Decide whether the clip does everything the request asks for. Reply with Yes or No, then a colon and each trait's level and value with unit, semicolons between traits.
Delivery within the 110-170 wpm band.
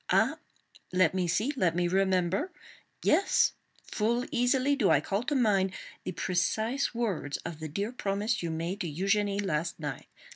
Yes: average, 160 wpm